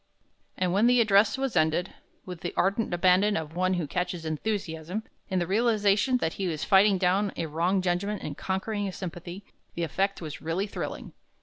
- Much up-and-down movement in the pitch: No, average, 3.0 semitones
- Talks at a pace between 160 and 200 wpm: Yes, average, 185 wpm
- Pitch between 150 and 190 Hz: Yes, medium, 185 Hz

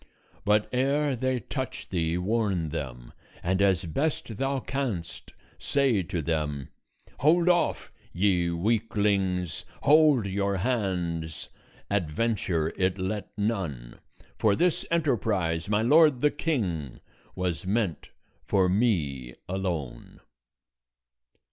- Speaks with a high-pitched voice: No, low, 100 Hz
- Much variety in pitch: Yes, wide, 6.4 semitones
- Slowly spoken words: Yes, slow, 105 wpm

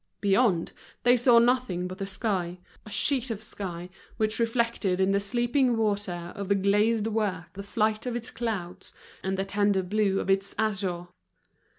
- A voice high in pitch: Yes, high, 205 Hz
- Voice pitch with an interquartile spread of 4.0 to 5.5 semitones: No, average, 3.1 semitones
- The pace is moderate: Yes, average, 170 wpm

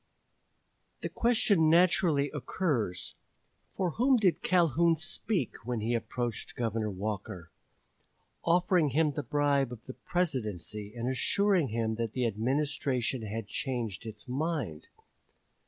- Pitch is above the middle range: No, low, 130 Hz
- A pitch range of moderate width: No, wide, 6.8 semitones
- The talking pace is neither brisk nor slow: No, slow, 120 wpm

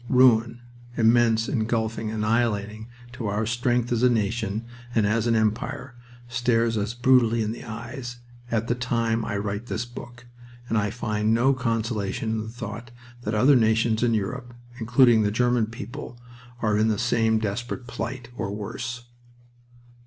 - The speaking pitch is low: Yes, low, 115 Hz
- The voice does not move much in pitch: Yes, narrow, 1.7 semitones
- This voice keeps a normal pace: Yes, average, 155 wpm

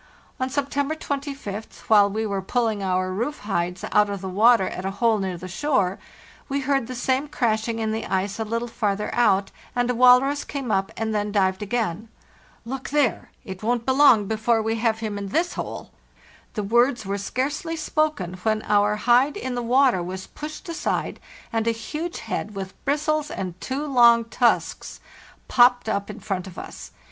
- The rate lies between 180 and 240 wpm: Yes, average, 185 wpm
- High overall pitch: Yes, high, 225 Hz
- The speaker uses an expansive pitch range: No, average, 4.6 semitones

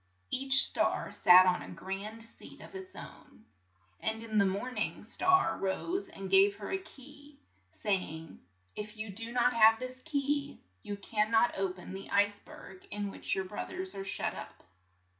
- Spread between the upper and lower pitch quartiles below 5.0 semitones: No, wide, 5.5 semitones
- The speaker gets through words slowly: No, average, 180 wpm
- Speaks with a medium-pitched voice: No, high, 215 Hz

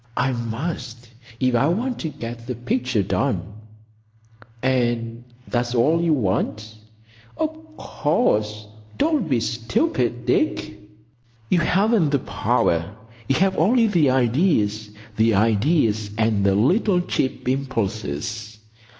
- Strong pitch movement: Yes, wide, 7.3 semitones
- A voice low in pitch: Yes, low, 120 Hz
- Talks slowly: Yes, slow, 115 wpm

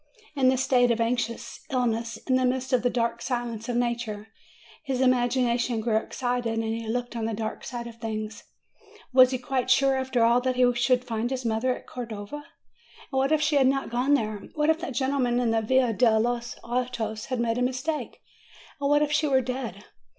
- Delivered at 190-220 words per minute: Yes, fast, 205 wpm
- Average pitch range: No, narrow, 2.1 semitones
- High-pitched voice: Yes, high, 245 Hz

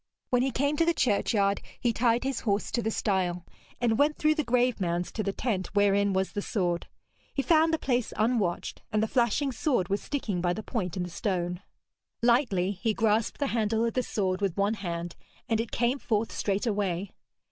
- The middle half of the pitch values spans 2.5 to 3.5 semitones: No, average, 4.2 semitones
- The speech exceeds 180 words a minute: Yes, average, 200 wpm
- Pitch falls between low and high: No, high, 215 Hz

